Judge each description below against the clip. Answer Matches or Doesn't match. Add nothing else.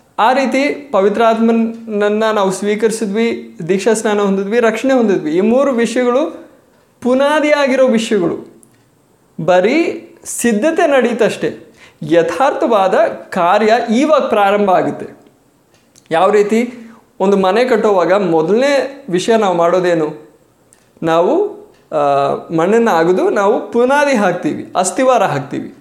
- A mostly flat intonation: Doesn't match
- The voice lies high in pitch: Matches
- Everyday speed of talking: Matches